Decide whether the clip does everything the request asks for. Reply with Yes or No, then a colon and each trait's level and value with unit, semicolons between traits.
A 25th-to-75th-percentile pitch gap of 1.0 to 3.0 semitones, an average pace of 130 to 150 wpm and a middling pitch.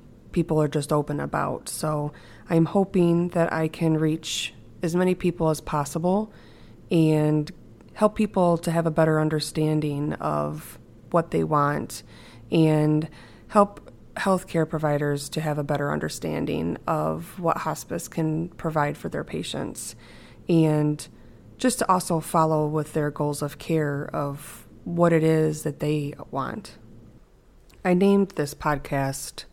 Yes: narrow, 2.5 semitones; slow, 135 wpm; medium, 155 Hz